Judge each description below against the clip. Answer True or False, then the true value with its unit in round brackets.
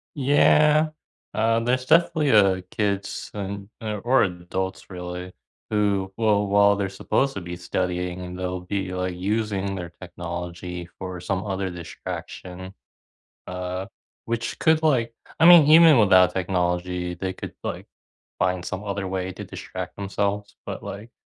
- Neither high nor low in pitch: False (95 Hz)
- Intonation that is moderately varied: True (3.0 semitones)